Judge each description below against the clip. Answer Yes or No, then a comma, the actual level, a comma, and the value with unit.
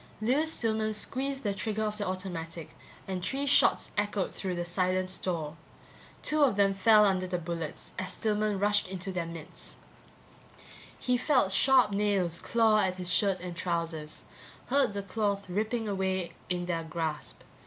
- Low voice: No, high, 195 Hz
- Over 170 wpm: No, average, 160 wpm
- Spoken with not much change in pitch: No, average, 3.4 semitones